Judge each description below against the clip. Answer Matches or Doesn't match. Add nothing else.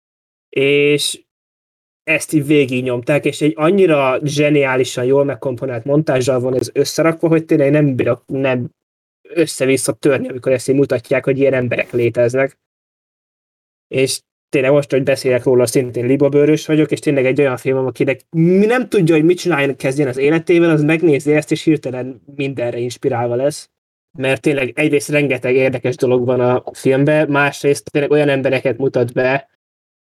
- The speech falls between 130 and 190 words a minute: Matches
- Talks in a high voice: Doesn't match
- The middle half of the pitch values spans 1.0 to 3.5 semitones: Matches